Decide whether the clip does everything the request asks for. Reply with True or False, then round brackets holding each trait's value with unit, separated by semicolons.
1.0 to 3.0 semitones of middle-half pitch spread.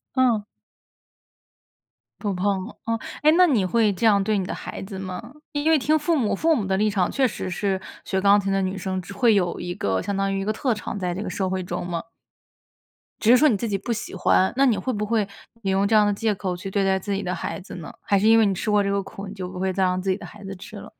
True (2.5 semitones)